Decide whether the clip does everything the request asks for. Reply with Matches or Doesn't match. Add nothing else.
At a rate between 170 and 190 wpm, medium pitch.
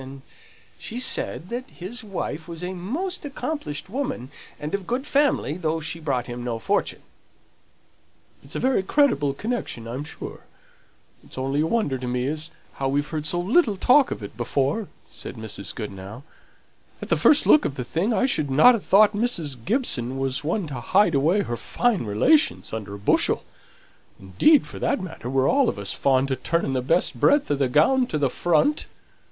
Matches